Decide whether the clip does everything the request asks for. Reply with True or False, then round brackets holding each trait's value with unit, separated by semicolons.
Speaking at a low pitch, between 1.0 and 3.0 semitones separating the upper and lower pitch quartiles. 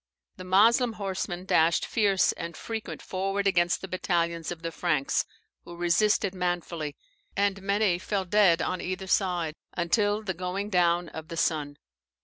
False (180 Hz; 2.7 semitones)